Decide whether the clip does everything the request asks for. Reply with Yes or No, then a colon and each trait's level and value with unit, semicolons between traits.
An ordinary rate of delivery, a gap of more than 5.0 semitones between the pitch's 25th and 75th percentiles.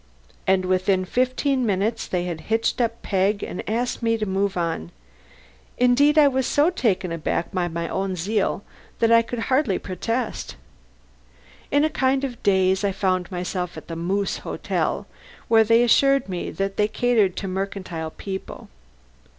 No: average, 160 wpm; average, 4.6 semitones